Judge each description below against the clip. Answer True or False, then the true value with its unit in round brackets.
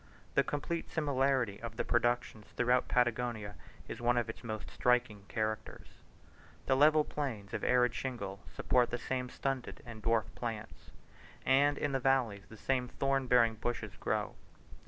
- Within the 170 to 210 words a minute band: False (155 wpm)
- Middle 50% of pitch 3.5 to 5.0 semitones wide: False (3.1 semitones)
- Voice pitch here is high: False (120 Hz)